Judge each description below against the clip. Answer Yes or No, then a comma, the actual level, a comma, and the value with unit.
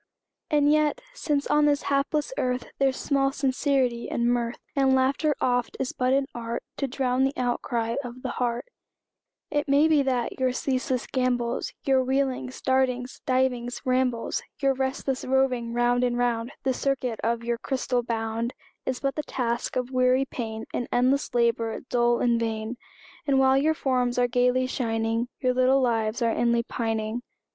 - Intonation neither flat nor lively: No, narrow, 2.0 semitones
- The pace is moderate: Yes, average, 165 wpm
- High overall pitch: Yes, very high, 255 Hz